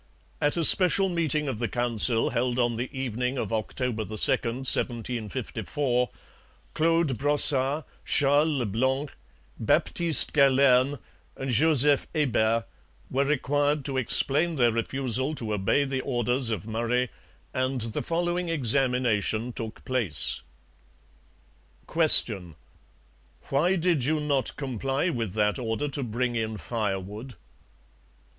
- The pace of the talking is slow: Yes, slow, 120 wpm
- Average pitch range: Yes, average, 3.9 semitones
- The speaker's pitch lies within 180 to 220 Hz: No, low, 130 Hz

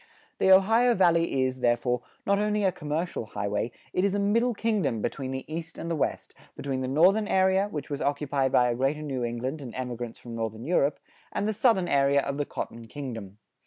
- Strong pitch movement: Yes, wide, 7.3 semitones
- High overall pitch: No, medium, 145 Hz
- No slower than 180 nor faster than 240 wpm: Yes, average, 200 wpm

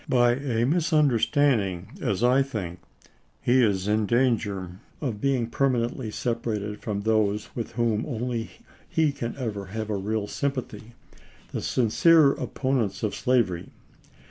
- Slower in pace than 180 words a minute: Yes, average, 145 wpm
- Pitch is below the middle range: Yes, low, 115 Hz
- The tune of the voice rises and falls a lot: No, average, 3.8 semitones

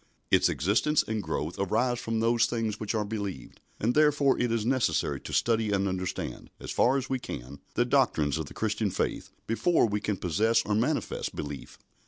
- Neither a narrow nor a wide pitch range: Yes, average, 3.7 semitones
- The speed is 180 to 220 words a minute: Yes, average, 190 wpm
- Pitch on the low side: Yes, low, 110 Hz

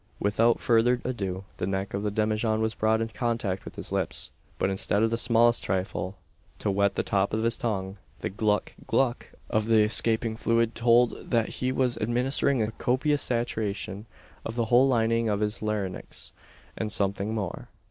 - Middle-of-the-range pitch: No, low, 110 Hz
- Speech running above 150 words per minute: Yes, average, 180 wpm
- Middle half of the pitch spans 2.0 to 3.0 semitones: Yes, narrow, 2.5 semitones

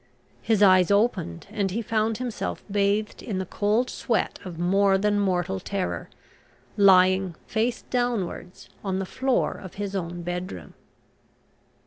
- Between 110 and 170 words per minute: Yes, slow, 135 wpm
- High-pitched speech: Yes, high, 200 Hz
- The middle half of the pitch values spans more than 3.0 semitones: No, average, 2.7 semitones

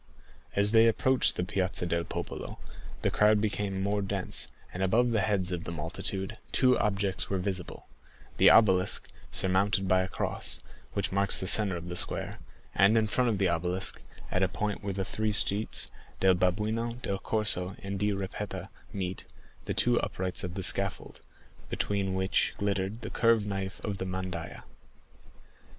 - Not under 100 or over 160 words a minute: No, average, 170 wpm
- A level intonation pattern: Yes, narrow, 2.1 semitones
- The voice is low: Yes, very low, 95 Hz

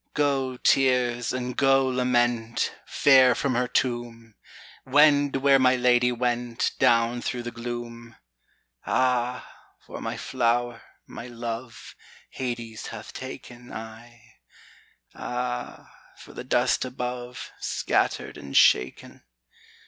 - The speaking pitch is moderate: No, low, 120 Hz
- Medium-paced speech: No, slow, 110 wpm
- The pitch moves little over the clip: Yes, narrow, 1.4 semitones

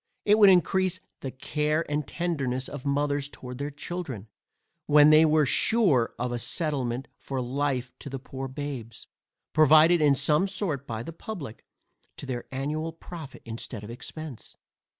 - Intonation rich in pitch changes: No, average, 3.4 semitones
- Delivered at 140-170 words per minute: Yes, average, 155 wpm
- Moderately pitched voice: Yes, medium, 145 Hz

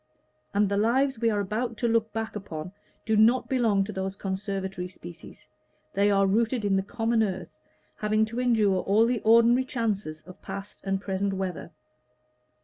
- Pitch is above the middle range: Yes, high, 205 Hz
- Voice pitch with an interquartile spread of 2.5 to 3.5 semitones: Yes, average, 2.9 semitones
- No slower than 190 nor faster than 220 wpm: No, average, 170 wpm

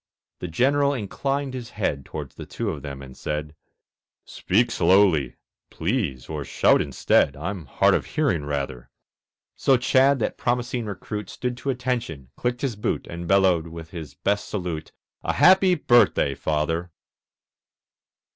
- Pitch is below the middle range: Yes, very low, 95 Hz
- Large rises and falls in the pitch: Yes, wide, 8.3 semitones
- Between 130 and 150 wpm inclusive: Yes, average, 145 wpm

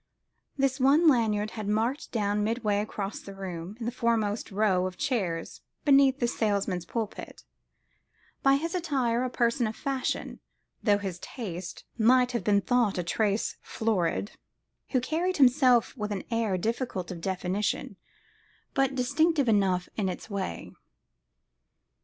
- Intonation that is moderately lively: Yes, average, 4.4 semitones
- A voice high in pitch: Yes, high, 220 Hz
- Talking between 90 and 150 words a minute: Yes, average, 140 wpm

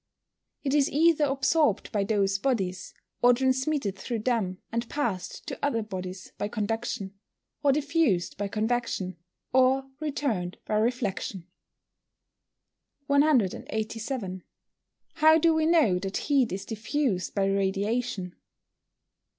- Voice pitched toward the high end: Yes, high, 230 Hz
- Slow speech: Yes, slow, 120 wpm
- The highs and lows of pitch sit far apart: Yes, wide, 5.8 semitones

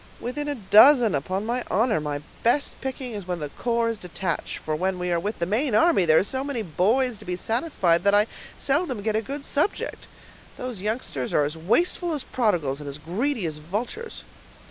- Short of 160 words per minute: No, fast, 205 wpm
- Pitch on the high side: Yes, high, 215 Hz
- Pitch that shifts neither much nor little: No, wide, 6.7 semitones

